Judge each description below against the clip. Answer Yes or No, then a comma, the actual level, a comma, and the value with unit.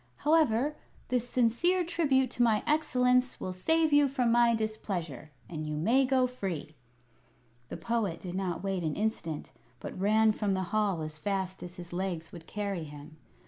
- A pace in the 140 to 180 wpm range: Yes, average, 170 wpm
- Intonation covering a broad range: Yes, wide, 6.2 semitones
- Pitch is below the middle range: No, high, 210 Hz